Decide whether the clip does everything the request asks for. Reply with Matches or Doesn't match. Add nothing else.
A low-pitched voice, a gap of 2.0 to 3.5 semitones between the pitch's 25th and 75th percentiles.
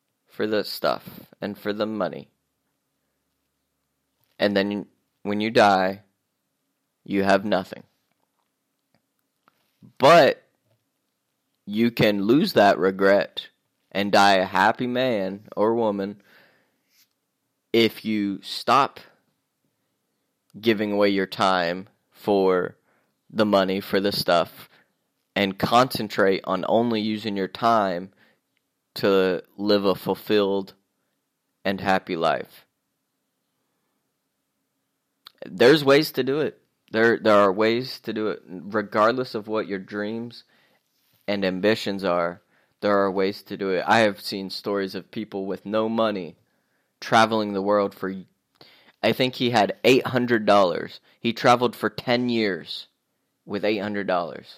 Matches